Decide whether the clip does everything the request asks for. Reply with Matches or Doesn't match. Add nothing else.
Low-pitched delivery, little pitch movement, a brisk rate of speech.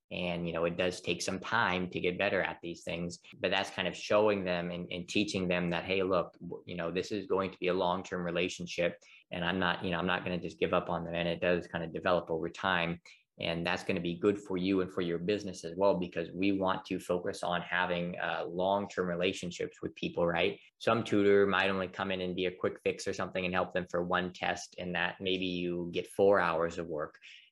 Matches